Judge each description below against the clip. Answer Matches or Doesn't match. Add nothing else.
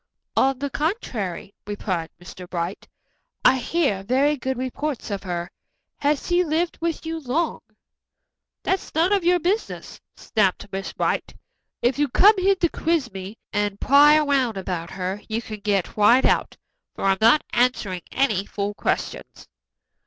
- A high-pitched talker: Matches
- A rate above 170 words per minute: Doesn't match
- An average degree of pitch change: Doesn't match